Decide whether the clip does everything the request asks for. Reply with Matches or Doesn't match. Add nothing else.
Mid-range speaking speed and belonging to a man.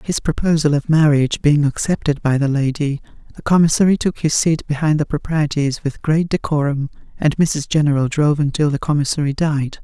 Doesn't match